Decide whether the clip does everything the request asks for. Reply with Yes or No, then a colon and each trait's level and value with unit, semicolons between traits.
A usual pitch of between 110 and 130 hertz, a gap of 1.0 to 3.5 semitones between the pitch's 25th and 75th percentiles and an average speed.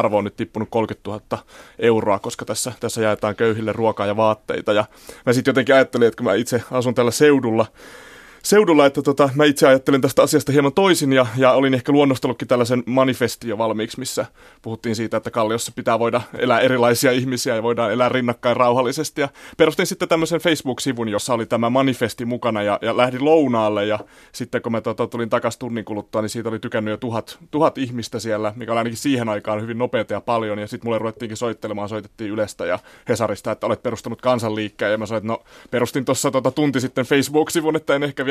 No: low, 120 Hz; average, 3.2 semitones; fast, 205 wpm